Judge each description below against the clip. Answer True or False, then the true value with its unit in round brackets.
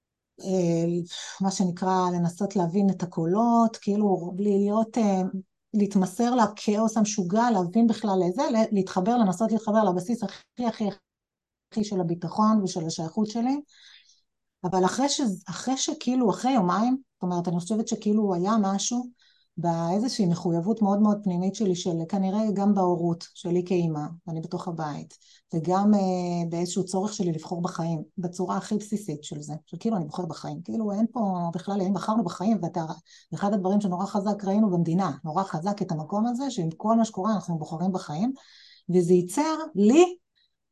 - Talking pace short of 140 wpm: False (150 wpm)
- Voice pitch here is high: True (195 Hz)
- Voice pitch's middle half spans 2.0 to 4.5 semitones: True (3.6 semitones)